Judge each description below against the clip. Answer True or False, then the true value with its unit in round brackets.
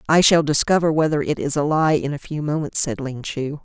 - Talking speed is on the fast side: True (245 wpm)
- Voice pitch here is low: False (150 Hz)